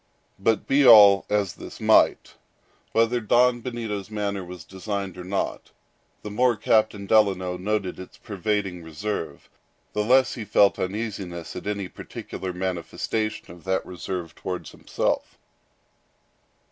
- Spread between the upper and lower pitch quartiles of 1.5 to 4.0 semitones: Yes, average, 2.8 semitones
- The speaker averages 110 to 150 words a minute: Yes, slow, 135 wpm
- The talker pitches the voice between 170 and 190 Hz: No, low, 100 Hz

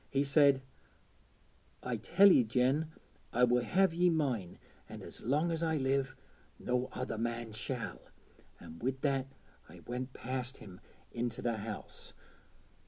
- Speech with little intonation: No, average, 3.3 semitones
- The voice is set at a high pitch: No, low, 130 Hz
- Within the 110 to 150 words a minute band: Yes, average, 145 wpm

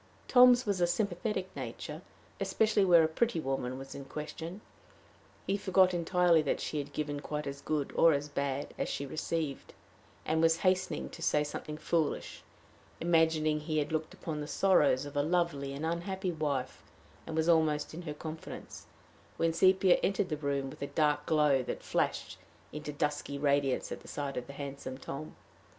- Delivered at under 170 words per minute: No, average, 175 wpm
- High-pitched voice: No, medium, 155 Hz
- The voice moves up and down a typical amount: Yes, average, 3.3 semitones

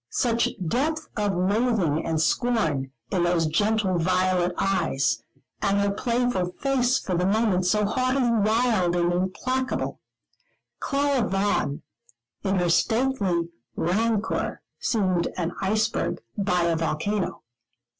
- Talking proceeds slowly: Yes, slow, 115 wpm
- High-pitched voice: Yes, high, 200 Hz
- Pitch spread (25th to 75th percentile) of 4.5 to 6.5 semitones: Yes, average, 4.8 semitones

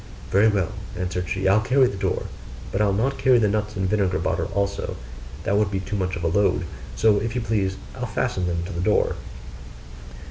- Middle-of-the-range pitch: No, low, 100 Hz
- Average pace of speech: No, fast, 210 wpm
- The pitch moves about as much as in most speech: No, narrow, 2.3 semitones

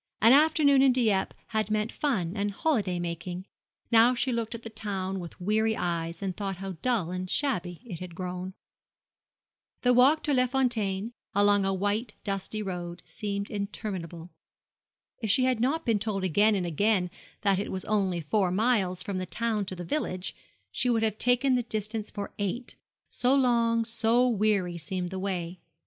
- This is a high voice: Yes, high, 205 Hz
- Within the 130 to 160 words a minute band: No, average, 175 wpm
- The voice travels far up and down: No, average, 4.1 semitones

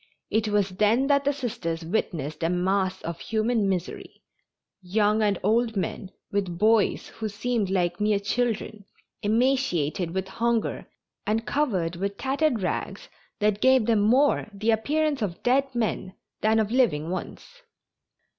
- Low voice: No, high, 215 Hz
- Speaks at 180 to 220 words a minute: No, average, 145 wpm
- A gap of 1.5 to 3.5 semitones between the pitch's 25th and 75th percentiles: No, average, 4.0 semitones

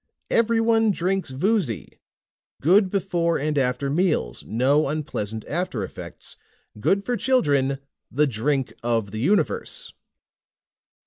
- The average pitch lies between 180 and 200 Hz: No, medium, 150 Hz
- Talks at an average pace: No, slow, 110 wpm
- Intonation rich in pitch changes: Yes, wide, 7.4 semitones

